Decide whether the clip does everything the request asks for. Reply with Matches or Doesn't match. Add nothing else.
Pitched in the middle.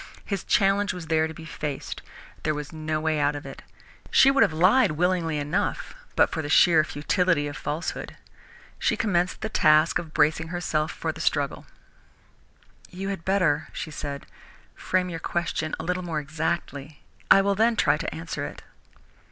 Matches